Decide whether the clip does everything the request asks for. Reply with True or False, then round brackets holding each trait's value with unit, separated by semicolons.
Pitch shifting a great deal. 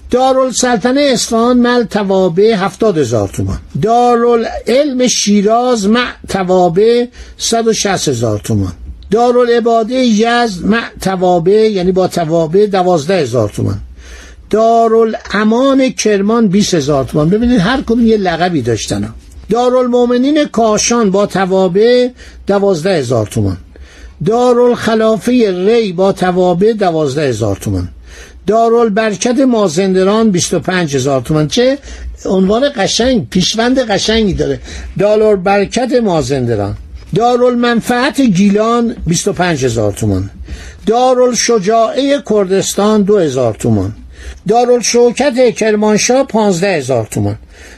True (7.2 semitones)